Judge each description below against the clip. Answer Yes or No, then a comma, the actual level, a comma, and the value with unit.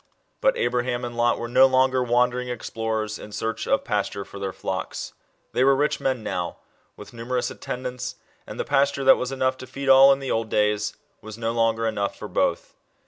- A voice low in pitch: Yes, low, 120 Hz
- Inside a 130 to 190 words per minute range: No, average, 200 wpm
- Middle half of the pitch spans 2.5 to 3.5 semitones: Yes, average, 3.0 semitones